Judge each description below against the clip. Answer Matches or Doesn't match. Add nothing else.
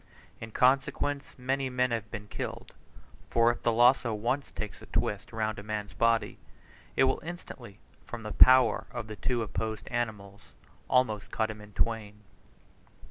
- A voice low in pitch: Matches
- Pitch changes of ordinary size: Matches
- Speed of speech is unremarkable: Matches